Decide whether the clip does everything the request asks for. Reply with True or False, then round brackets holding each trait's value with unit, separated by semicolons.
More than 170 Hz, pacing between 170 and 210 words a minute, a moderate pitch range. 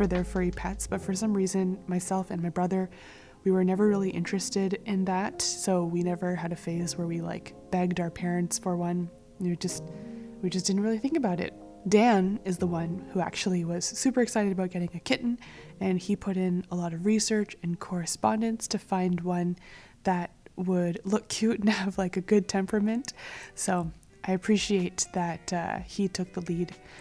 False (185 Hz; 190 wpm; 2.3 semitones)